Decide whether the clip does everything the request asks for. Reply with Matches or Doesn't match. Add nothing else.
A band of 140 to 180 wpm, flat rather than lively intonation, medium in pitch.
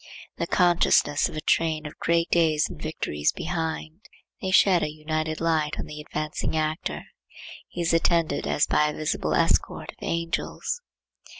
Matches